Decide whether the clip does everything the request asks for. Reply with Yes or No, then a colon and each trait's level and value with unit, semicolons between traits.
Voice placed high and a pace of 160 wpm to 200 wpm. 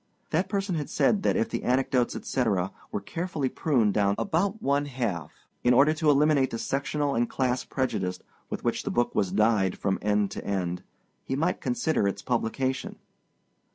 No: low, 130 Hz; average, 175 wpm